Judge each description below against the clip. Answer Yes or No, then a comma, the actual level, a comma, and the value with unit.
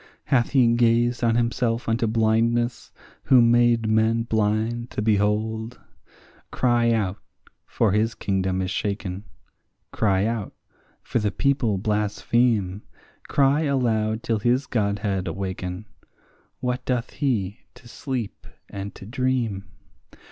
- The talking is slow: Yes, slow, 120 wpm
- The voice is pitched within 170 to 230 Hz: No, low, 115 Hz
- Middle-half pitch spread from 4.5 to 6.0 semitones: No, narrow, 2.6 semitones